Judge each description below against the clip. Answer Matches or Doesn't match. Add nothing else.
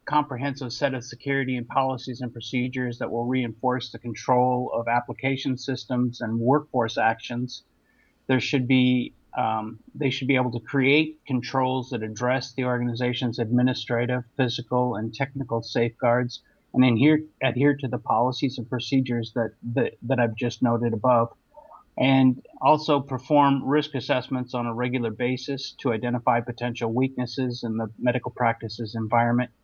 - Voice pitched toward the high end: Doesn't match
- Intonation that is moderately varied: Doesn't match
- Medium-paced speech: Matches